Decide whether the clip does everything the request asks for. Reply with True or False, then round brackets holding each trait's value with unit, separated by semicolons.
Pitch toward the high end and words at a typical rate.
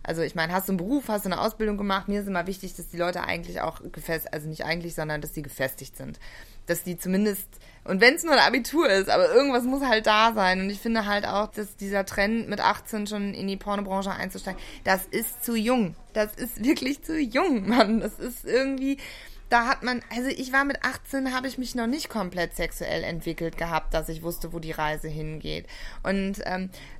False (200 Hz; 220 wpm)